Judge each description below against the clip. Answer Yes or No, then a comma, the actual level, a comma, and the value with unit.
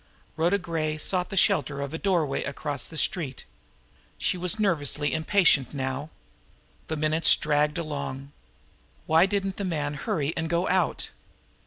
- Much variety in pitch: No, average, 3.4 semitones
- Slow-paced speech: No, average, 145 wpm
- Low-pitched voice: No, medium, 155 Hz